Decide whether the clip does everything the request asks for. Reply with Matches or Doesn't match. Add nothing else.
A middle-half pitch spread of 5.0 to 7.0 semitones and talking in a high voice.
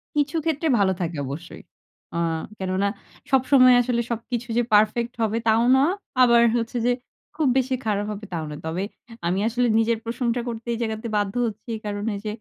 Doesn't match